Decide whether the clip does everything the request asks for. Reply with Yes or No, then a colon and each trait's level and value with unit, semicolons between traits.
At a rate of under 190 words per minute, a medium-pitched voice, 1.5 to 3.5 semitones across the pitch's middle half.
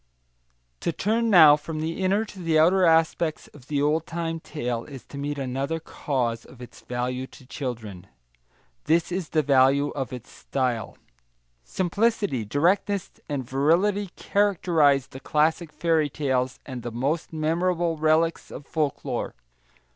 No: average, 145 wpm; medium, 150 Hz; average, 4.3 semitones